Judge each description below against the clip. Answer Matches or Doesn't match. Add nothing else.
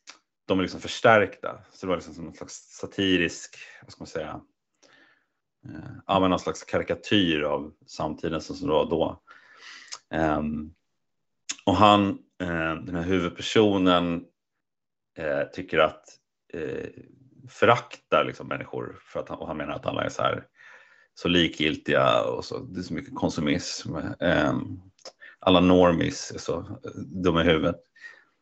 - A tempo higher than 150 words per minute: Doesn't match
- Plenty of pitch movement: Matches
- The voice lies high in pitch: Doesn't match